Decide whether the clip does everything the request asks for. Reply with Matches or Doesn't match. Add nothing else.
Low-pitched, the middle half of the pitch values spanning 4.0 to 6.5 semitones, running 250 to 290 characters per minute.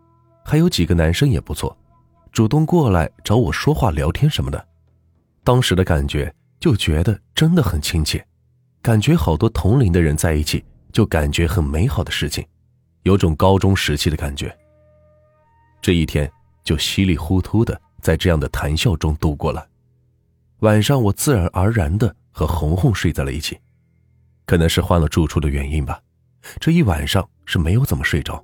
Matches